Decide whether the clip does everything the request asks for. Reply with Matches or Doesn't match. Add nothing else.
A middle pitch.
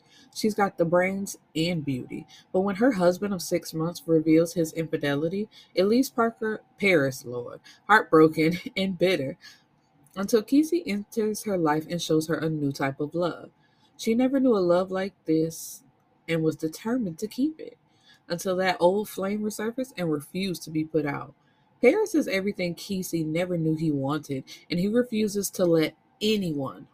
Matches